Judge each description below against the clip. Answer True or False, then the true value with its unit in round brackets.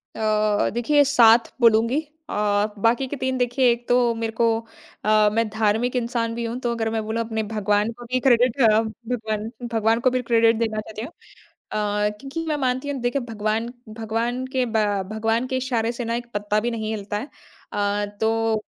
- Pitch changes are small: True (2.1 semitones)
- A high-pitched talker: True (230 Hz)